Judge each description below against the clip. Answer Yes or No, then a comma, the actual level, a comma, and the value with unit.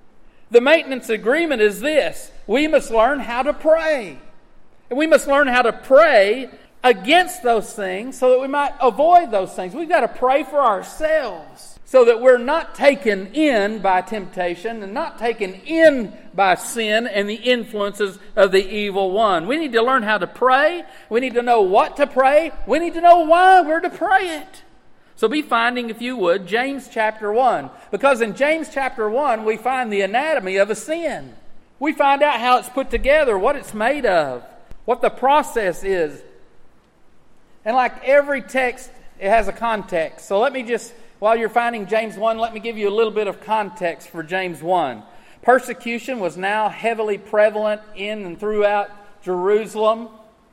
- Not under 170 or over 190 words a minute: Yes, average, 180 wpm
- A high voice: Yes, high, 235 Hz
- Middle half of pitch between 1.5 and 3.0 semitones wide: No, average, 5.1 semitones